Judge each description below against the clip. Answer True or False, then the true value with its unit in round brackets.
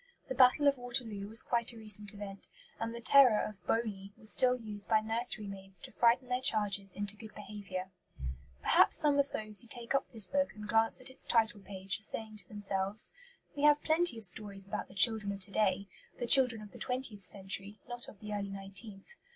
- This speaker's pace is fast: True (210 wpm)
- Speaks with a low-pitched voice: False (215 Hz)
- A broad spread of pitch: False (3.3 semitones)